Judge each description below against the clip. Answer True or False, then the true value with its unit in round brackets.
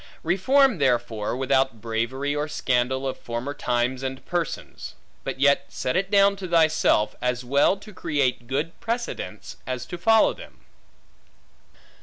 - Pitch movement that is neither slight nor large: False (6.0 semitones)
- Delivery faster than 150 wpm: False (140 wpm)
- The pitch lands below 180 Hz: True (140 Hz)